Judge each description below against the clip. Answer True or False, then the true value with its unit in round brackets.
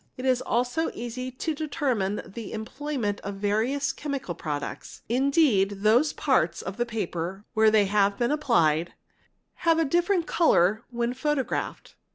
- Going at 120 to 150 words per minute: True (145 wpm)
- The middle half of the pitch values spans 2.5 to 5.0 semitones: False (5.6 semitones)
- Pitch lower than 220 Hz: False (240 Hz)